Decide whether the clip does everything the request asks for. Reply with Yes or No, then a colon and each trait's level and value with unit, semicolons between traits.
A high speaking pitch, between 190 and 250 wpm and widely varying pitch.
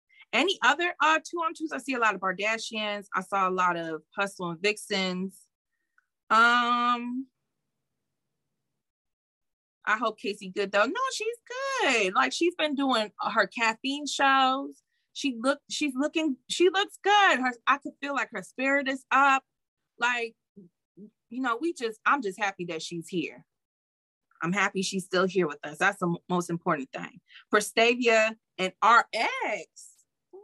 No: high, 225 Hz; average, 160 wpm; wide, 6.6 semitones